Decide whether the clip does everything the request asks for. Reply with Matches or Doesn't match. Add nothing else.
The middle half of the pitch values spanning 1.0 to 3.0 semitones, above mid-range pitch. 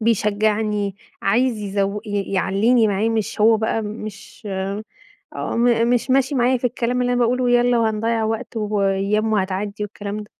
Matches